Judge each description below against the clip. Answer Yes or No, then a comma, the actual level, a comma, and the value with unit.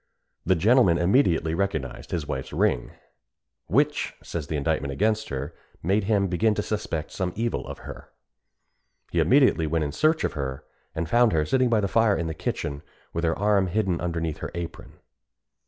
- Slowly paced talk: No, average, 175 wpm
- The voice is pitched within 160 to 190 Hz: No, very low, 85 Hz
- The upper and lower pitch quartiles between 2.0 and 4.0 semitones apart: No, average, 5.0 semitones